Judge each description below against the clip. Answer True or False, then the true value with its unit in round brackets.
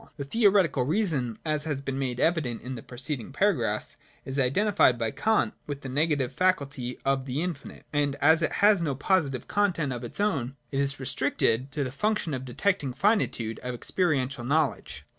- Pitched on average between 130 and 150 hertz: True (140 Hz)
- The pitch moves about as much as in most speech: True (4.8 semitones)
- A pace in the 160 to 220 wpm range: True (180 wpm)